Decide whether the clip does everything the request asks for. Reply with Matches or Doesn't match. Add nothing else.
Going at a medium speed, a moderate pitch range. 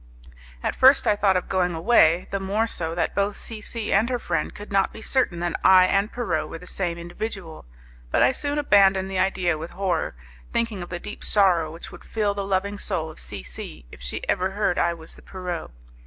Doesn't match